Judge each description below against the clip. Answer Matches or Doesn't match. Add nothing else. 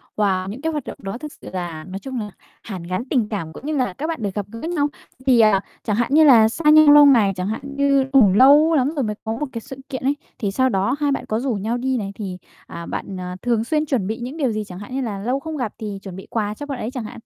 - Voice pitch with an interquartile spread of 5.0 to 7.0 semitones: Matches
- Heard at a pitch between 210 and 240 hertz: Matches